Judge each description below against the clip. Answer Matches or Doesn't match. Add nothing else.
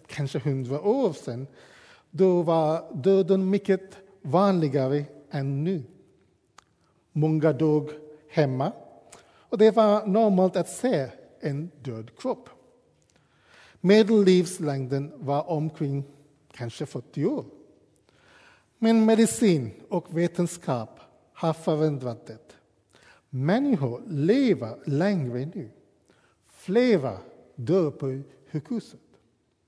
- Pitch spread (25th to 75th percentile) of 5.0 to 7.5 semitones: Matches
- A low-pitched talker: Doesn't match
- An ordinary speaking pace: Doesn't match